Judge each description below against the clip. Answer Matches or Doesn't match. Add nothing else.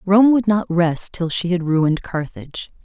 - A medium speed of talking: Matches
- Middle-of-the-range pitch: Matches